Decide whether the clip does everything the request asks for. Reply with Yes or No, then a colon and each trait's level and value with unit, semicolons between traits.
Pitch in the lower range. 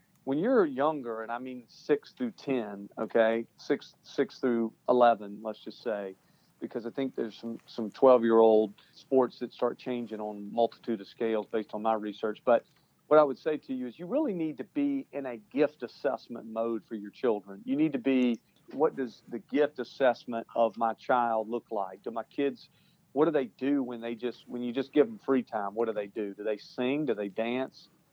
Yes: low, 120 Hz